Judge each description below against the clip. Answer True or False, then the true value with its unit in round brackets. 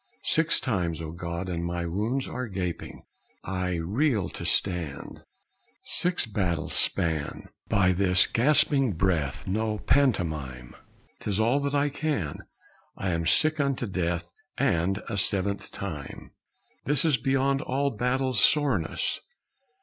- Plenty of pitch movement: True (7.6 semitones)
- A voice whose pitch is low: True (100 Hz)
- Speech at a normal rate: False (125 wpm)